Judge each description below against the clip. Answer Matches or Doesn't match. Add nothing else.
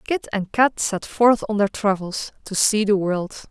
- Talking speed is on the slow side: Doesn't match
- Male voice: Doesn't match